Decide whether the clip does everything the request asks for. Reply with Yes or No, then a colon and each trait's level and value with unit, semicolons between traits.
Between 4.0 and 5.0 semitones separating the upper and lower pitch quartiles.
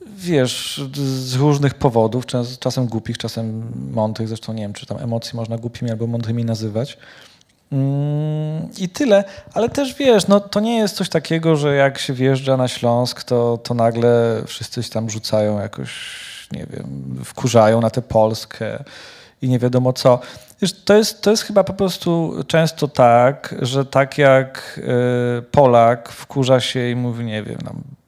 Yes: average, 4.6 semitones